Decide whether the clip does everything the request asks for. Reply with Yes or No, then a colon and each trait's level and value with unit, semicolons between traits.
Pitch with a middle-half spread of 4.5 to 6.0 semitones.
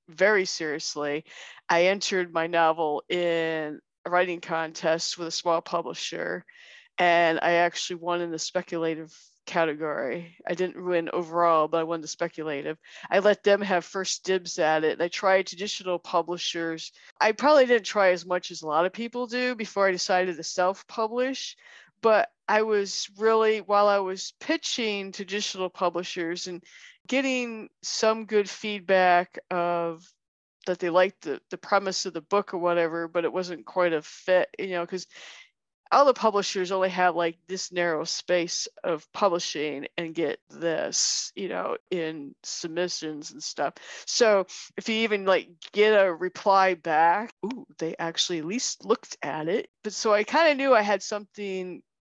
No: average, 3.4 semitones